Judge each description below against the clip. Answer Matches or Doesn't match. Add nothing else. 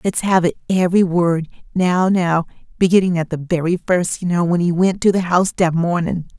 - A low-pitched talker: Doesn't match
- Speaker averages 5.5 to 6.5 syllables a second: Doesn't match